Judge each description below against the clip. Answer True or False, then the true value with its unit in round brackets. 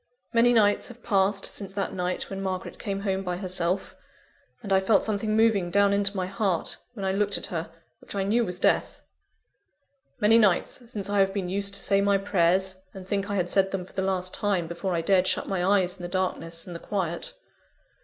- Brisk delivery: True (215 wpm)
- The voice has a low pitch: False (195 Hz)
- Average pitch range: False (1.8 semitones)